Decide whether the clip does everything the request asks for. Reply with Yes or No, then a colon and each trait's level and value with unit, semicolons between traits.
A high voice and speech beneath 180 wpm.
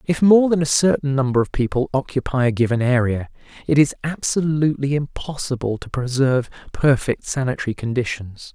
No: low, 135 Hz; average, 150 wpm